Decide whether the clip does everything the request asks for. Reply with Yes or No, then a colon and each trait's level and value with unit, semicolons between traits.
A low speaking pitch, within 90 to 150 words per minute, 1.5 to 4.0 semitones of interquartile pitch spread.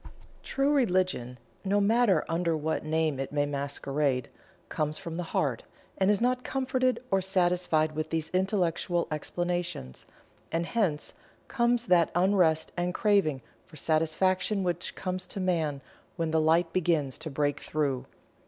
No: medium, 170 Hz; average, 145 wpm; average, 3.6 semitones